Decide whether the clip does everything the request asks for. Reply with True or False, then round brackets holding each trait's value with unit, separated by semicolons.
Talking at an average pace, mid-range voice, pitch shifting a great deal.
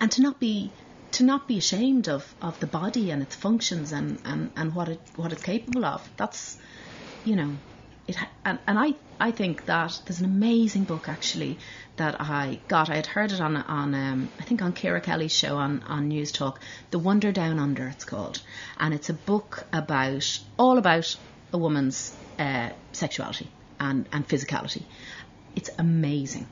True (185 wpm; 160 Hz; 6.2 semitones)